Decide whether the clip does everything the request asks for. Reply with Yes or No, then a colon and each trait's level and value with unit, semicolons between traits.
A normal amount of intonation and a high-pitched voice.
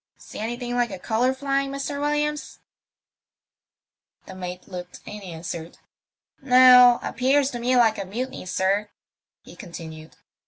No: wide, 5.9 semitones; high, 240 Hz